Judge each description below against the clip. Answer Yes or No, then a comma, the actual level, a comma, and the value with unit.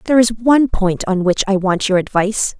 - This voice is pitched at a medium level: No, high, 210 Hz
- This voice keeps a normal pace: No, fast, 230 wpm